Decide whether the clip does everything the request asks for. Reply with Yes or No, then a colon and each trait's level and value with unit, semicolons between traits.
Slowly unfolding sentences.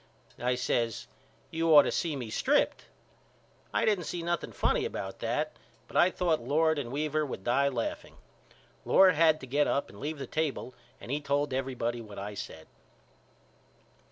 No: average, 170 wpm